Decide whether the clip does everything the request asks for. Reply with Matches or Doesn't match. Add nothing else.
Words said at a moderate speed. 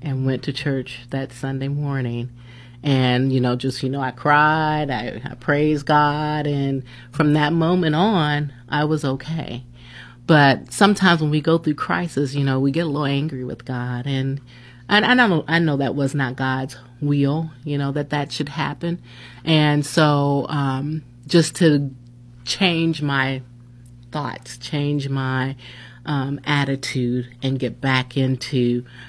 Matches